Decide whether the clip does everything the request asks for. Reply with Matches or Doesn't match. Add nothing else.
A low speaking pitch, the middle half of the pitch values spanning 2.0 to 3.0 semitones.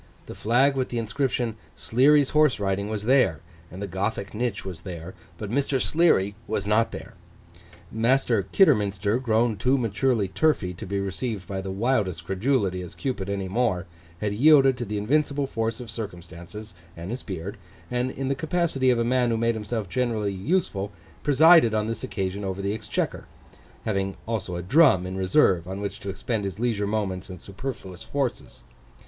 Doesn't match